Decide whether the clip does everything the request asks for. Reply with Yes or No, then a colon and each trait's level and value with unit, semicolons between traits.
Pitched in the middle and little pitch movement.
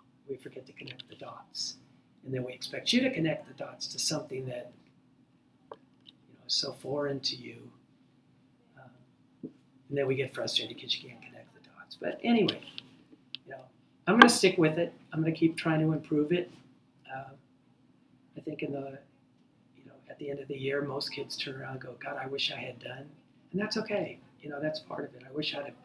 No: medium, 145 Hz; average, 3.4 semitones